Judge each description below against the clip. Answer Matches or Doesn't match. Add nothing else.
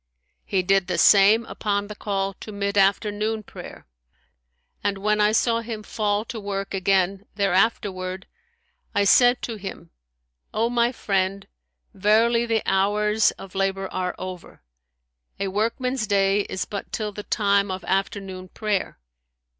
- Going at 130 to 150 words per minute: Matches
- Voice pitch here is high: Matches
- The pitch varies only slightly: Matches